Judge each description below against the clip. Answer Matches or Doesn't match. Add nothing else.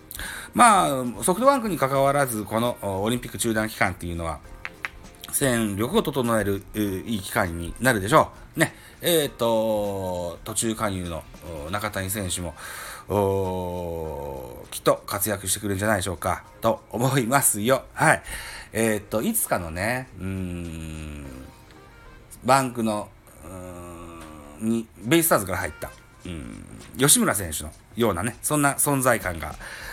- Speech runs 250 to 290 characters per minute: Matches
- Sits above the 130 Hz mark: Doesn't match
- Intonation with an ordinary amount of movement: Matches